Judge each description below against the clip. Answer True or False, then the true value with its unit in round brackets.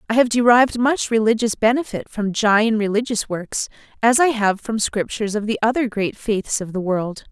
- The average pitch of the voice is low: False (220 Hz)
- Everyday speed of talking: True (190 wpm)